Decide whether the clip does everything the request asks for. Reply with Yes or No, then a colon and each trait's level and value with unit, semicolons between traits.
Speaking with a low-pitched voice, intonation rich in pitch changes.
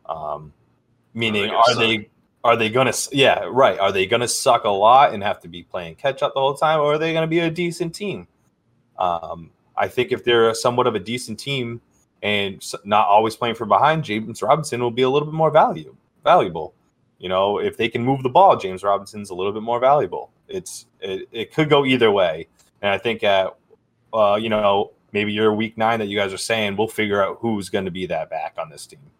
Yes: low, 115 Hz; wide, 6.1 semitones